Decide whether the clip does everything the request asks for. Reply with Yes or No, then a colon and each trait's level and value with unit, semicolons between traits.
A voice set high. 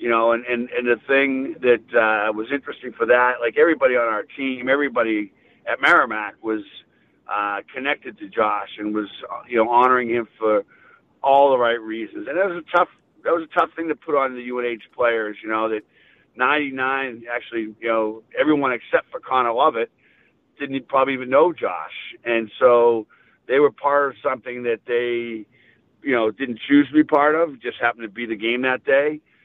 No: low, 120 Hz